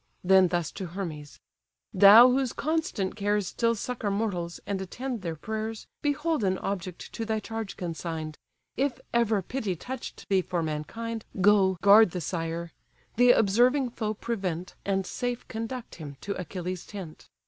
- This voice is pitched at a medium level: No, high, 200 Hz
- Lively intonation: No, average, 4.3 semitones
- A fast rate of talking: No, average, 150 wpm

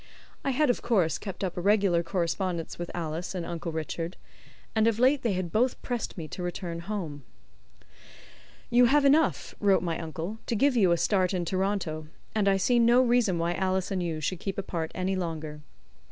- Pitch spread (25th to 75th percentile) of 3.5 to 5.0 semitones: Yes, average, 4.5 semitones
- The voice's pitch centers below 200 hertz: Yes, medium, 185 Hz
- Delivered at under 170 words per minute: No, average, 195 wpm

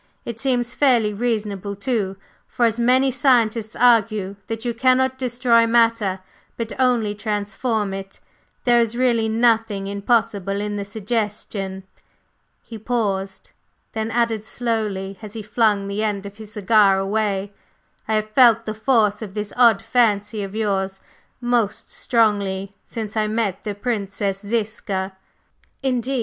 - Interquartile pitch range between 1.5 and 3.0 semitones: Yes, average, 2.7 semitones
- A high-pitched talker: Yes, high, 215 Hz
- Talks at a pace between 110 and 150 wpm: Yes, average, 140 wpm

